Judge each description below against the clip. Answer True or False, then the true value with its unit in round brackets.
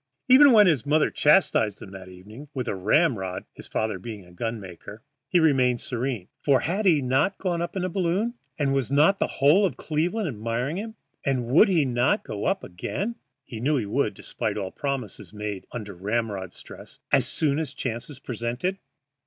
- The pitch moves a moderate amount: False (7.5 semitones)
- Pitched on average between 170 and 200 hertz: False (130 Hz)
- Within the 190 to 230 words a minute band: True (200 wpm)